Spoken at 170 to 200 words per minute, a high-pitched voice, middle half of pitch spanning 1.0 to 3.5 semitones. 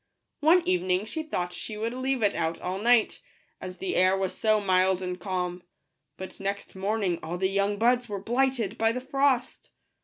No: average, 185 wpm; high, 200 Hz; average, 4.5 semitones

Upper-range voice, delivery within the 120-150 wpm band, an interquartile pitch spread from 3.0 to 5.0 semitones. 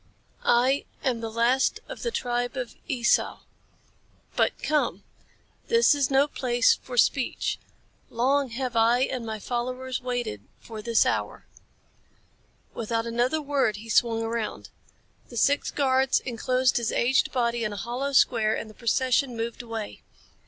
No: high, 245 Hz; average, 145 wpm; narrow, 2.4 semitones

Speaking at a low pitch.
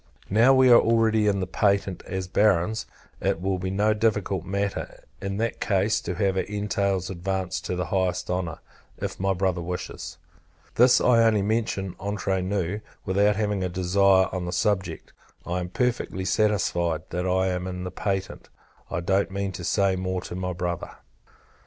Yes: very low, 95 Hz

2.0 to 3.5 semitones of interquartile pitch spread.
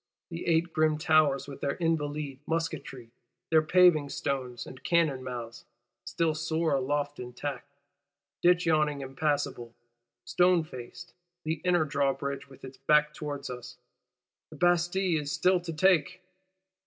Yes: average, 3.1 semitones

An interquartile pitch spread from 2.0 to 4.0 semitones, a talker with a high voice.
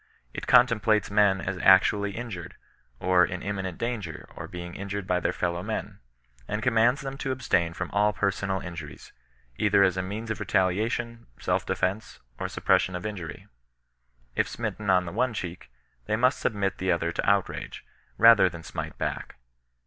No: average, 3.3 semitones; low, 100 Hz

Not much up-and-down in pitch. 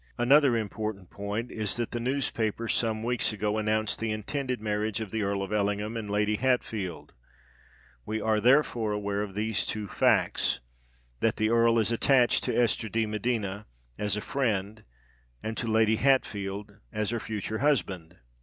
Yes: narrow, 2.2 semitones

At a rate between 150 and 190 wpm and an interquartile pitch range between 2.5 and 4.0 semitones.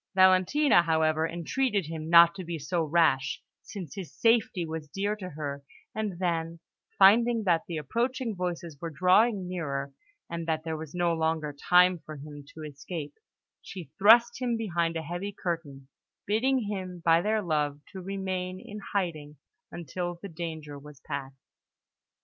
Yes: average, 155 wpm; average, 3.6 semitones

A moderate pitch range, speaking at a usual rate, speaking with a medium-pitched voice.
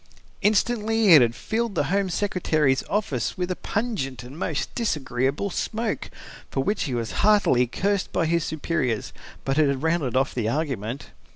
No: wide, 7.3 semitones; average, 165 wpm; medium, 160 Hz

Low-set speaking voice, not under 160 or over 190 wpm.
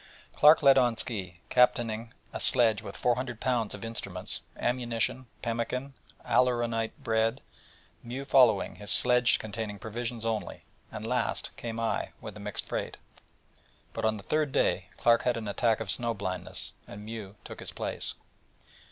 No: low, 115 Hz; average, 150 wpm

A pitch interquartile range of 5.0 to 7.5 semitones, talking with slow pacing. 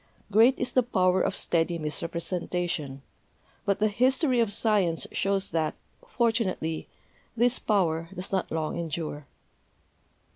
Yes: average, 5.3 semitones; slow, 120 wpm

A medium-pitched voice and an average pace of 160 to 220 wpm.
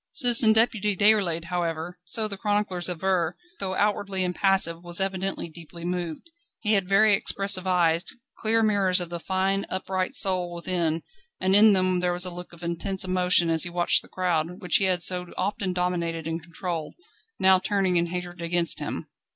Yes: medium, 180 Hz; average, 175 wpm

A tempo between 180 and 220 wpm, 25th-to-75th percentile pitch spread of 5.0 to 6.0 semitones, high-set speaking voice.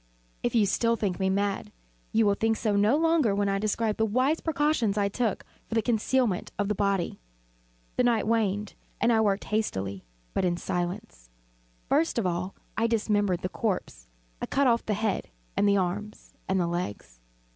No: average, 185 wpm; average, 3.2 semitones; high, 210 Hz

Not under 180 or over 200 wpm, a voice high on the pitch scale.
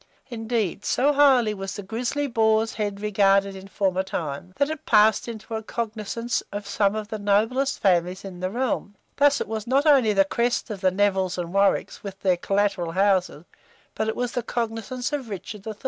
Yes: average, 195 wpm; high, 210 Hz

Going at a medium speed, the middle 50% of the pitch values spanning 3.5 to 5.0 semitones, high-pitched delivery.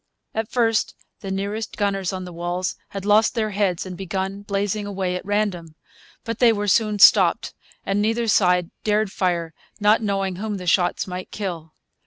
No: average, 175 wpm; narrow, 2.6 semitones; high, 195 Hz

